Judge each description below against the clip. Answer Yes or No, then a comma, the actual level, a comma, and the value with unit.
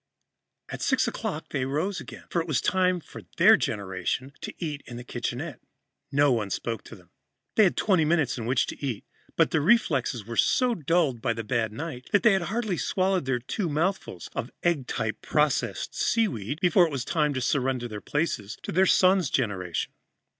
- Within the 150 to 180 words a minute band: No, average, 195 wpm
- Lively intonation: Yes, wide, 6.9 semitones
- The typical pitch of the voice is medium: Yes, medium, 145 Hz